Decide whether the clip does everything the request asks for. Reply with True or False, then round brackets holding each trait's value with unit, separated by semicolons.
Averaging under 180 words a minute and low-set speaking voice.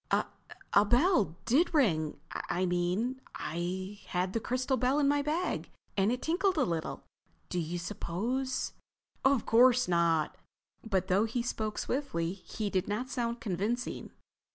False (145 wpm; 220 Hz)